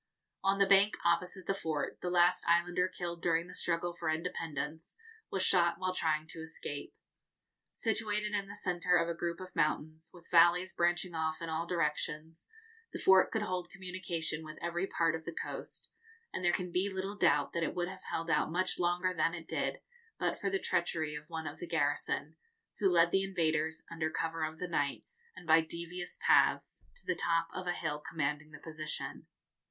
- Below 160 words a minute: No, average, 195 wpm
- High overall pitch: No, medium, 170 Hz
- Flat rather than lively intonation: Yes, narrow, 2.2 semitones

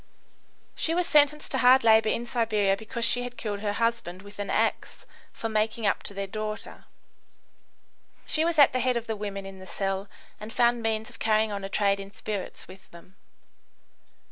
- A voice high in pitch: Yes, high, 215 Hz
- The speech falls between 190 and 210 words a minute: Yes, average, 195 wpm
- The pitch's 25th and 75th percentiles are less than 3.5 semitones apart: Yes, average, 3.0 semitones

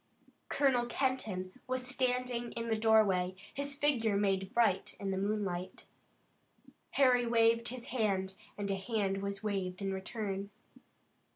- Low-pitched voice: No, high, 215 Hz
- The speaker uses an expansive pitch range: No, average, 4.0 semitones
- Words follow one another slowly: Yes, slow, 130 wpm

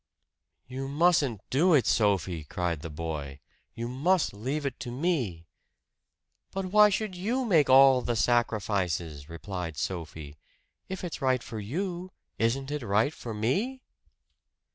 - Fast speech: No, average, 140 wpm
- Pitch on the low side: Yes, low, 125 Hz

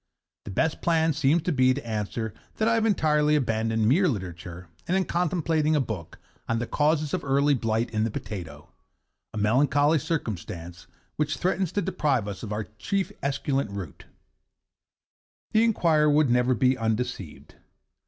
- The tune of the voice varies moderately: No, wide, 6.2 semitones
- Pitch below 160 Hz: Yes, low, 135 Hz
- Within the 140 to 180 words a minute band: Yes, average, 160 wpm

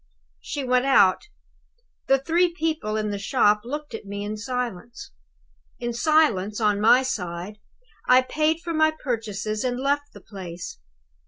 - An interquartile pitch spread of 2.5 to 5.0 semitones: No, wide, 5.6 semitones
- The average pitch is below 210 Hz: No, high, 240 Hz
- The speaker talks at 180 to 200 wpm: No, average, 150 wpm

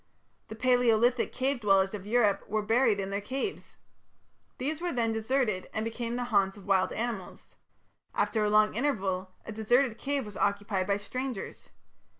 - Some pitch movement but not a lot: Yes, average, 3.5 semitones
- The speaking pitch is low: No, high, 220 Hz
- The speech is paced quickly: No, average, 160 wpm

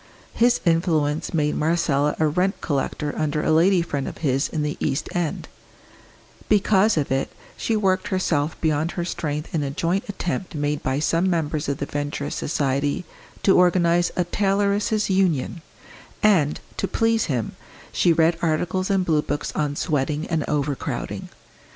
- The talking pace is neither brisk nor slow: Yes, average, 155 wpm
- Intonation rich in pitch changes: No, average, 4.0 semitones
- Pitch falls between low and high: Yes, medium, 160 Hz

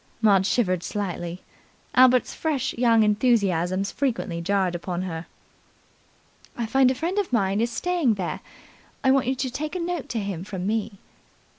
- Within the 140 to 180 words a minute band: Yes, average, 160 wpm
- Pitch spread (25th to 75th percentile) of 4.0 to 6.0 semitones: Yes, wide, 5.5 semitones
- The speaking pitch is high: Yes, high, 220 Hz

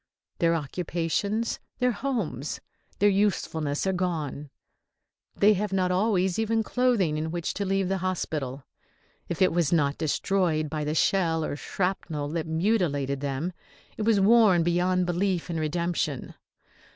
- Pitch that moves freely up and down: No, average, 3.9 semitones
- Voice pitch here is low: No, medium, 175 Hz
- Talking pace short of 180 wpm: Yes, average, 140 wpm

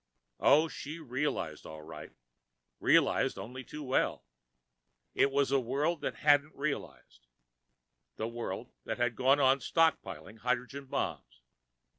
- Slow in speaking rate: Yes, slow, 125 wpm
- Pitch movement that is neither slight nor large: Yes, average, 3.6 semitones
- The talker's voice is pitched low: Yes, low, 130 Hz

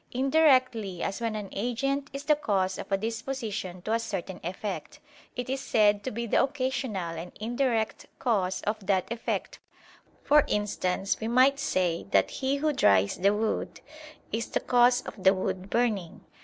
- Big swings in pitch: No, average, 4.9 semitones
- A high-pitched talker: Yes, high, 220 Hz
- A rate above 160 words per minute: Yes, average, 170 wpm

